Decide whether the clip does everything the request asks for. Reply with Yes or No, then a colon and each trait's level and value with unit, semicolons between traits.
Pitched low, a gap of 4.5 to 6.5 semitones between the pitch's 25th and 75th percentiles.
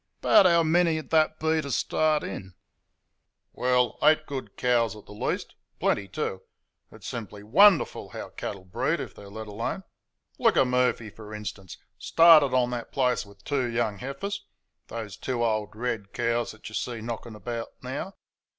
Yes: low, 120 Hz; average, 5.2 semitones